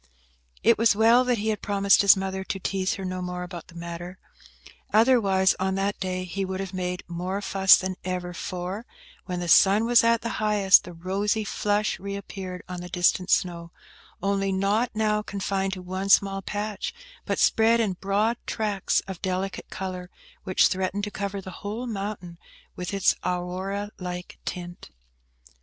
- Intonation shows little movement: Yes, narrow, 2.1 semitones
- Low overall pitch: No, high, 195 Hz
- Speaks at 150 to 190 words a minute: Yes, average, 175 wpm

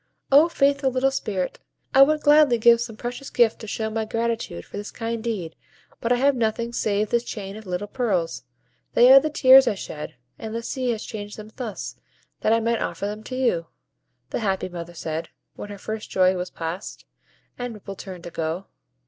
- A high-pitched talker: Yes, high, 220 Hz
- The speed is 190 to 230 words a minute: Yes, average, 200 wpm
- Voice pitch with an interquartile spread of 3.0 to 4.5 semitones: Yes, average, 4.2 semitones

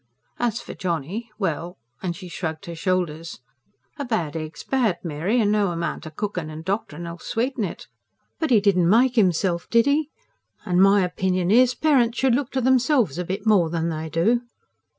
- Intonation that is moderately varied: No, wide, 5.7 semitones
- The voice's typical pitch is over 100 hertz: Yes, high, 190 Hz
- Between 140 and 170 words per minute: No, average, 185 wpm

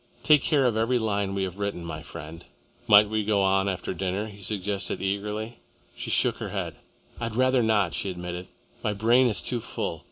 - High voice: No, low, 105 Hz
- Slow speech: No, average, 195 wpm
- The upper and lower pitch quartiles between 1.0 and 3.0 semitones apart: Yes, narrow, 2.5 semitones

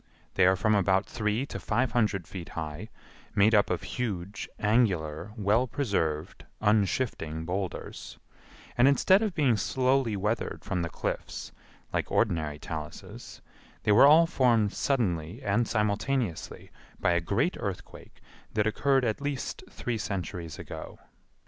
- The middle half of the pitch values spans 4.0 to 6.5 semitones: Yes, wide, 5.4 semitones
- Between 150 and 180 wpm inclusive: No, slow, 135 wpm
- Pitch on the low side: Yes, low, 105 Hz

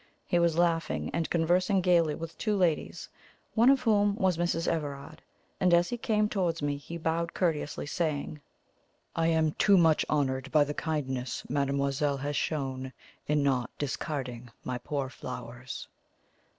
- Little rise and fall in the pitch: No, average, 3.7 semitones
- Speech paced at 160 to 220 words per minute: No, average, 150 wpm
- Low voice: No, medium, 155 Hz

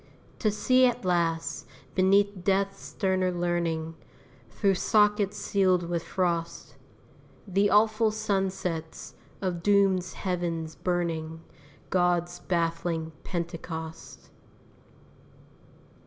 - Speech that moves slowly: Yes, slow, 85 wpm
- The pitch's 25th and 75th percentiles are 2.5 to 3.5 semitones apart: Yes, average, 2.8 semitones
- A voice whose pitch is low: No, medium, 180 Hz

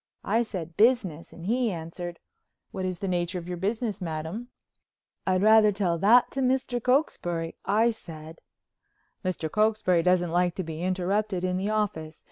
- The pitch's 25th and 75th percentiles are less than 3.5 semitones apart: No, average, 4.0 semitones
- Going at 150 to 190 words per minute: Yes, average, 160 wpm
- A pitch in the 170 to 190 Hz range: Yes, medium, 185 Hz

